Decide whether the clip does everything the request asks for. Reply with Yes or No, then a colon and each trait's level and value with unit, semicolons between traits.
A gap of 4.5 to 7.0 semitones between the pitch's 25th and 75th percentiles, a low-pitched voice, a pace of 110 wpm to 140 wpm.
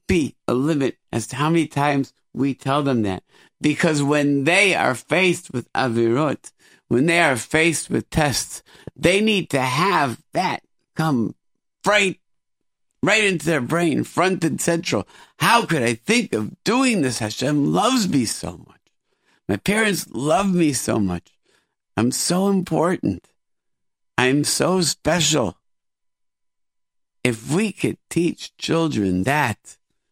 No: average, 5.2 semitones; medium, 155 Hz; slow, 135 wpm